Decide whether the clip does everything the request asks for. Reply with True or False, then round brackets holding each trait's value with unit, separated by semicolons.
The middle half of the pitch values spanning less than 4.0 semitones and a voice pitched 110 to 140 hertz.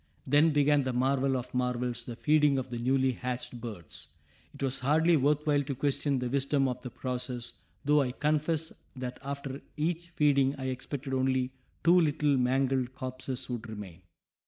True (2.5 semitones; 135 Hz)